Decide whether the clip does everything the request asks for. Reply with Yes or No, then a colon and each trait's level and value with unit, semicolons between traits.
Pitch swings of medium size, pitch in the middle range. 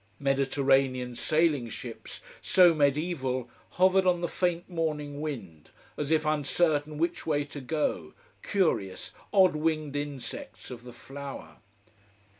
Yes: average, 3.4 semitones; medium, 145 Hz